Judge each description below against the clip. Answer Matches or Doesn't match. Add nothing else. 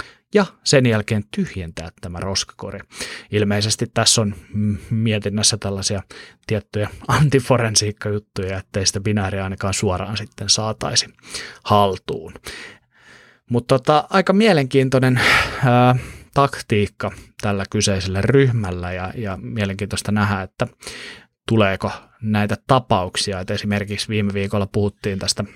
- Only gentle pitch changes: Doesn't match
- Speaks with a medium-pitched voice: Doesn't match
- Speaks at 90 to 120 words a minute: Matches